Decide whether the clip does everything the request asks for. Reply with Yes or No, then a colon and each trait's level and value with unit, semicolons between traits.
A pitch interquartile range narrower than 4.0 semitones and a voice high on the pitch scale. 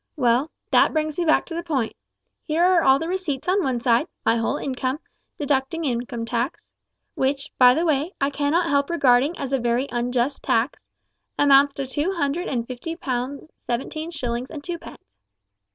No: average, 4.3 semitones; very high, 275 Hz